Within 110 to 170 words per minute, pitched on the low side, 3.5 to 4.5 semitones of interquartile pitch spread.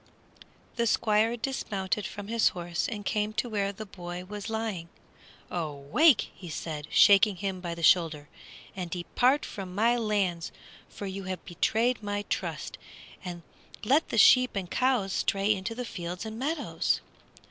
No: average, 160 wpm; high, 200 Hz; average, 3.9 semitones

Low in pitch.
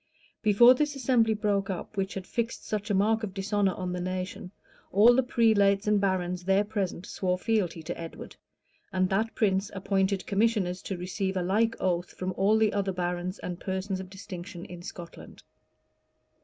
No: high, 195 Hz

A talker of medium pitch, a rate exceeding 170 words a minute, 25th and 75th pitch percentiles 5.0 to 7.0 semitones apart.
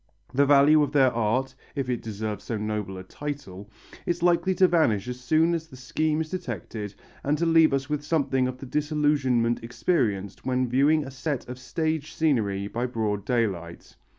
No: low, 130 Hz; average, 180 wpm; average, 5.3 semitones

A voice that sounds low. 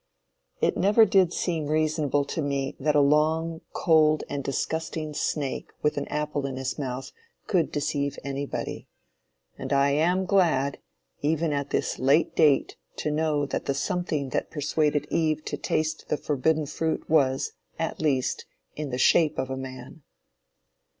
No: medium, 150 Hz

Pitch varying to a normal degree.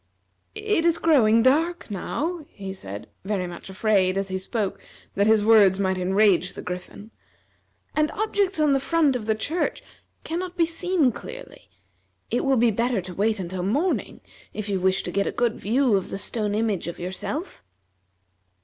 No: wide, 8.0 semitones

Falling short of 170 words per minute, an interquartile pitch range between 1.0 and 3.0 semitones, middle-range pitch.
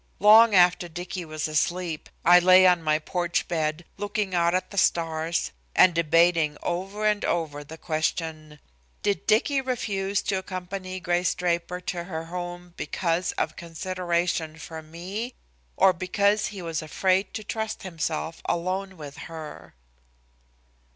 Yes: average, 140 wpm; narrow, 2.6 semitones; medium, 175 Hz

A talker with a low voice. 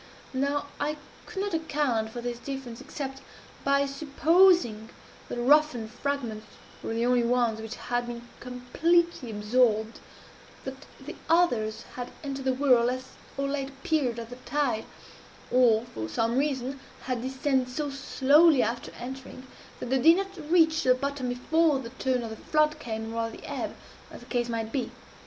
No: very high, 255 Hz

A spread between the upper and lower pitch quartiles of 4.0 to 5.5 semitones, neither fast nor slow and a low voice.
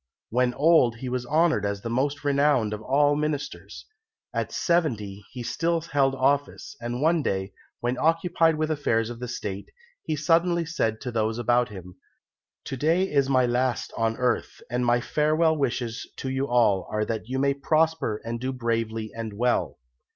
Yes: average, 4.7 semitones; average, 175 wpm; low, 125 Hz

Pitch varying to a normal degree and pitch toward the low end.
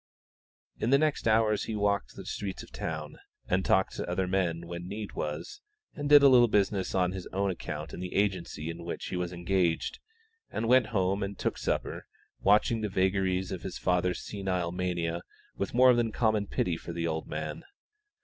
Yes: average, 3.3 semitones; very low, 95 Hz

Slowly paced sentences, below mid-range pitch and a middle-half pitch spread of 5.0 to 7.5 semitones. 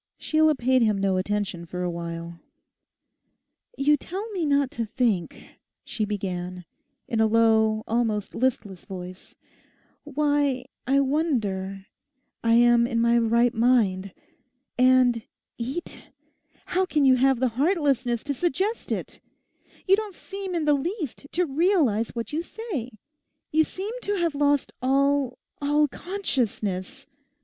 No: slow, 130 wpm; very high, 255 Hz; wide, 5.6 semitones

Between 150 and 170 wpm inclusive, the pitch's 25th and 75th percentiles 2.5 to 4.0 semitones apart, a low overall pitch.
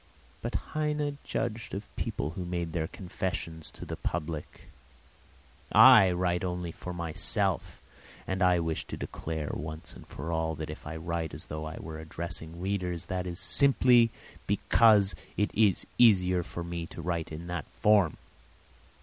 Yes: average, 160 wpm; average, 3.0 semitones; very low, 85 Hz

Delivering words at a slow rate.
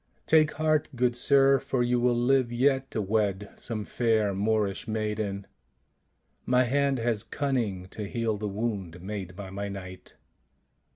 No: average, 155 wpm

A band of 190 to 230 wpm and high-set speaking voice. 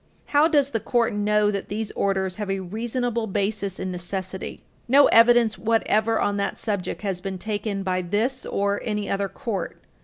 No: average, 175 wpm; high, 205 Hz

